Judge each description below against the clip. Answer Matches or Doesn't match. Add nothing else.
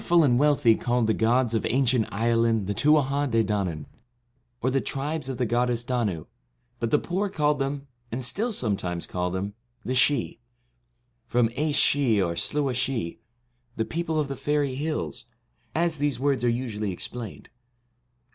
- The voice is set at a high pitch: Doesn't match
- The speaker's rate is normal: Matches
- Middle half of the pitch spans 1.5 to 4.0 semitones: Doesn't match